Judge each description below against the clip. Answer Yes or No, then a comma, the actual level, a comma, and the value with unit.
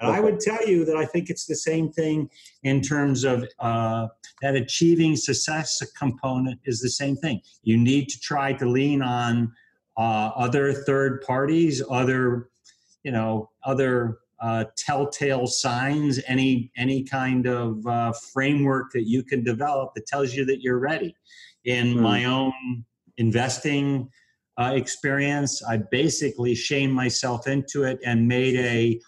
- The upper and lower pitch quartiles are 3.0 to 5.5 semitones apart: No, narrow, 2.6 semitones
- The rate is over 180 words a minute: No, average, 150 wpm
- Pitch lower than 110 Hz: No, low, 130 Hz